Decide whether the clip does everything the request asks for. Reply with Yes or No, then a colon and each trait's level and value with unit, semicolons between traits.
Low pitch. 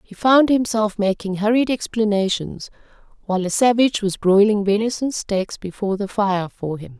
No: high, 210 Hz